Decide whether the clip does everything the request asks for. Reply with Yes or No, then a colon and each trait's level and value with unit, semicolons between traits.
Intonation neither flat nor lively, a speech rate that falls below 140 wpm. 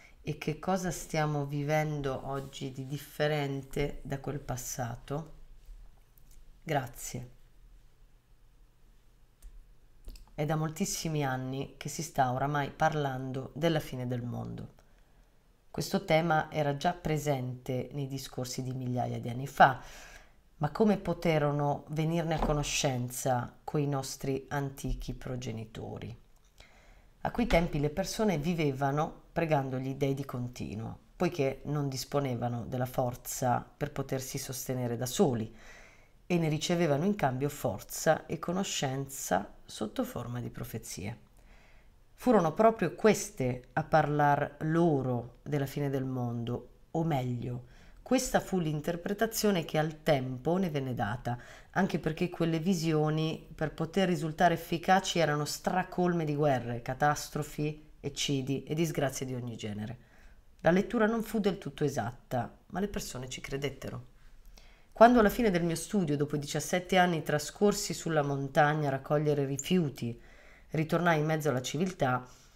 Yes: average, 4.1 semitones; average, 125 wpm